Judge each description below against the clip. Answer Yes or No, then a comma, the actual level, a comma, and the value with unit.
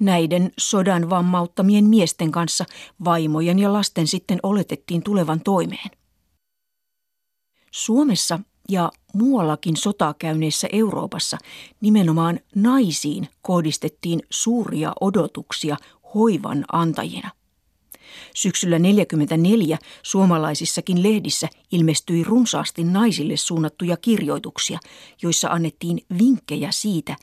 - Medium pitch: Yes, medium, 180 Hz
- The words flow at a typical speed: No, slow, 85 wpm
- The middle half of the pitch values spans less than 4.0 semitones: No, average, 4.3 semitones